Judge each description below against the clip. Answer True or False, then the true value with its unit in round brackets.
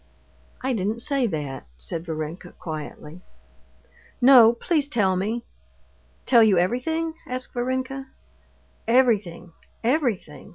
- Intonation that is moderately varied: False (6.6 semitones)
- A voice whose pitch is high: True (230 Hz)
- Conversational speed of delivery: False (100 wpm)